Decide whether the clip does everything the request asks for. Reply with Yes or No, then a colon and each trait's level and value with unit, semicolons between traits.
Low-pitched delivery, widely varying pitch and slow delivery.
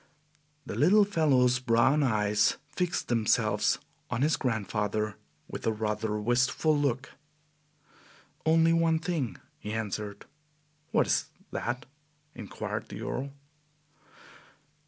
Yes: low, 125 Hz; wide, 6.0 semitones; slow, 105 wpm